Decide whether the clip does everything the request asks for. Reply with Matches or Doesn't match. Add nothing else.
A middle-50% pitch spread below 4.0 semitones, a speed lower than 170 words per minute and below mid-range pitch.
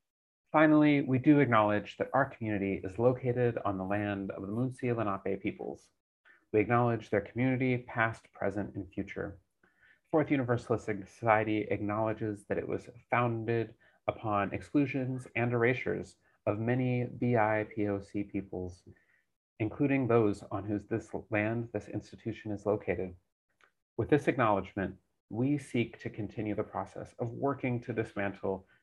Matches